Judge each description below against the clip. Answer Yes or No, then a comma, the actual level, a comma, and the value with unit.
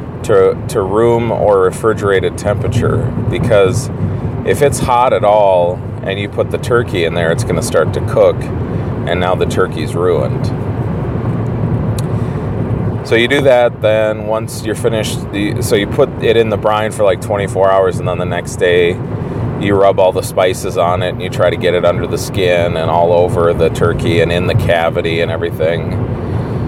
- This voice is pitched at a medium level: No, low, 110 Hz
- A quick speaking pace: No, average, 185 wpm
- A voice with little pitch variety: No, average, 3.9 semitones